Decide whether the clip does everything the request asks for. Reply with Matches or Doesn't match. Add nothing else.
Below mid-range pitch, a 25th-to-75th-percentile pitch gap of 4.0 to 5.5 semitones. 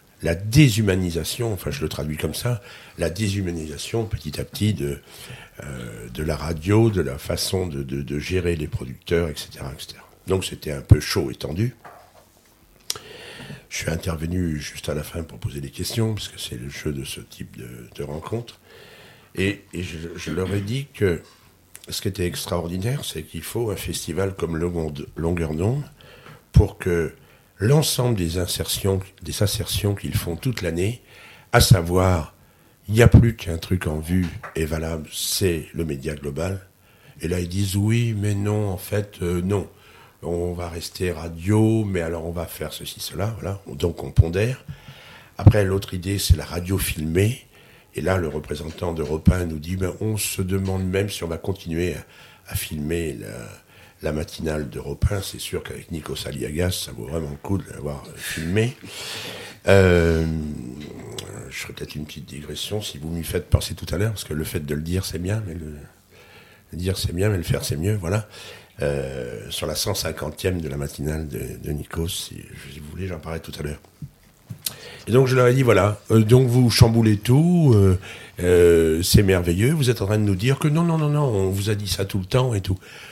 Matches